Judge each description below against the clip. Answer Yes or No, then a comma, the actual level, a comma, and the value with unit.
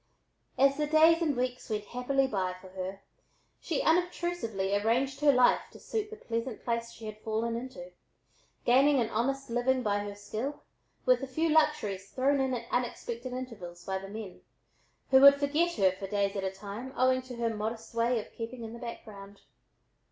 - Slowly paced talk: No, average, 185 wpm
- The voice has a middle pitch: No, high, 235 Hz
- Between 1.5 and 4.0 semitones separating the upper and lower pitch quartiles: No, average, 4.6 semitones